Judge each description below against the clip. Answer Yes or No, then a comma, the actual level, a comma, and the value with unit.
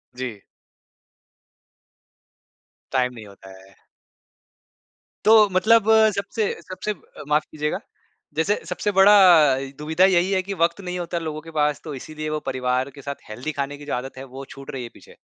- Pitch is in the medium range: Yes, medium, 155 Hz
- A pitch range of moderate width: No, wide, 5.8 semitones